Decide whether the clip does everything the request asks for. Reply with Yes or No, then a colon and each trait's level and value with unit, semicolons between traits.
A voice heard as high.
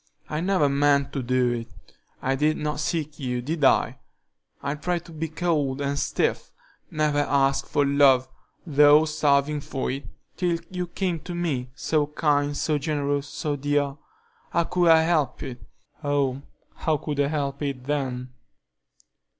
No: medium, 145 Hz